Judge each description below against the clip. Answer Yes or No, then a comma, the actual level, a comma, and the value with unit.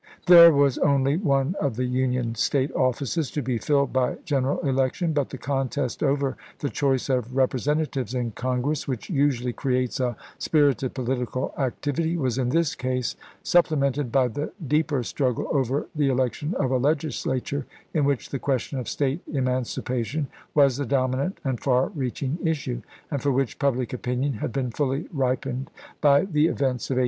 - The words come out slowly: No, average, 175 wpm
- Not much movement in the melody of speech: Yes, narrow, 2.3 semitones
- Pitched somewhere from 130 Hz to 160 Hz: Yes, low, 135 Hz